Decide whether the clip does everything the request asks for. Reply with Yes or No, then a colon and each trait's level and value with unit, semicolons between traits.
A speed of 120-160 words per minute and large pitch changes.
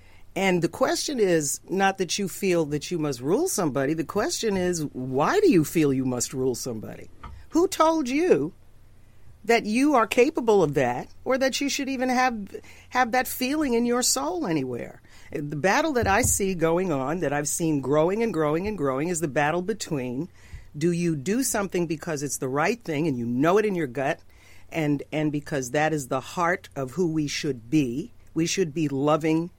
No: average, 195 wpm; wide, 7.7 semitones